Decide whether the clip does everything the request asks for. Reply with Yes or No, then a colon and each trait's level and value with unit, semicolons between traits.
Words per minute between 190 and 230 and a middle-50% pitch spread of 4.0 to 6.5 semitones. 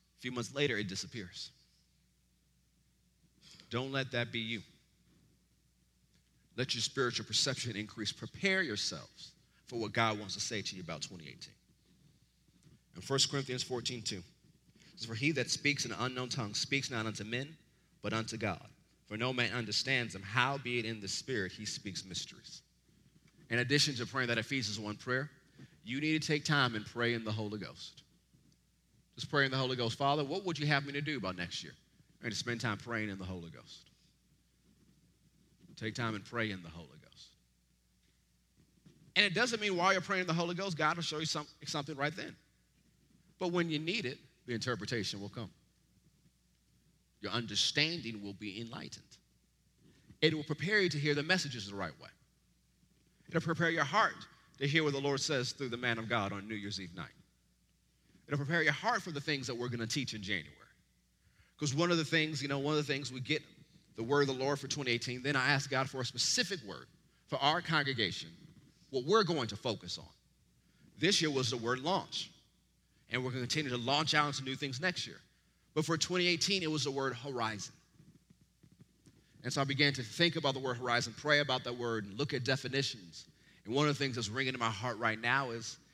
Yes: average, 200 wpm; average, 5.1 semitones